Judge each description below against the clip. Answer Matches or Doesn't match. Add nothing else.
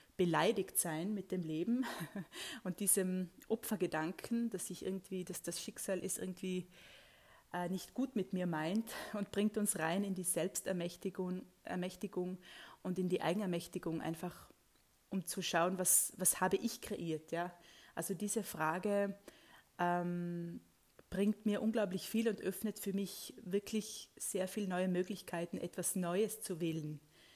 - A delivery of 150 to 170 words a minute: Doesn't match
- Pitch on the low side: Doesn't match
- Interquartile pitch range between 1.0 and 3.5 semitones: Matches